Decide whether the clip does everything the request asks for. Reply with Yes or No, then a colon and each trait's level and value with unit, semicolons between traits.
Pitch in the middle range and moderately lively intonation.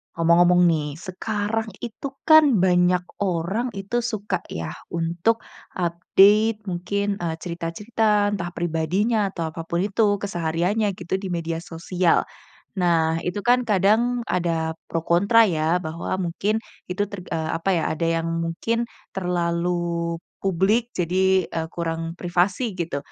Yes: medium, 180 Hz; average, 3.5 semitones